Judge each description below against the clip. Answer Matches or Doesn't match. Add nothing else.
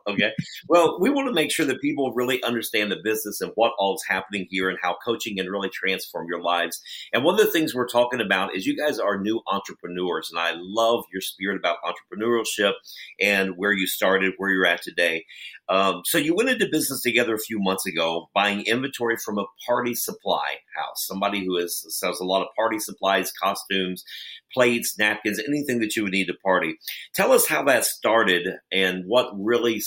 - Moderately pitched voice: Doesn't match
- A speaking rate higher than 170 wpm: Matches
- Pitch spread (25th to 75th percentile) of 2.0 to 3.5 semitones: Doesn't match